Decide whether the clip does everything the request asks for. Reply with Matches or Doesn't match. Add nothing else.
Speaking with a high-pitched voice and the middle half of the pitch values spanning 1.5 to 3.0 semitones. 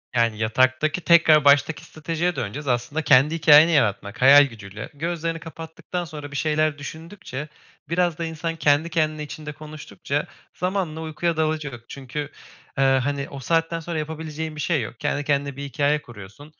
Doesn't match